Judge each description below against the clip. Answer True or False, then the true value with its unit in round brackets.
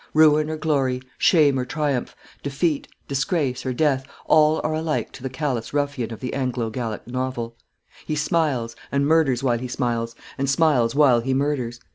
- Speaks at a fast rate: False (170 wpm)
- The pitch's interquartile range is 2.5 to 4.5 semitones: True (3.5 semitones)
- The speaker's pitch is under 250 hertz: True (135 Hz)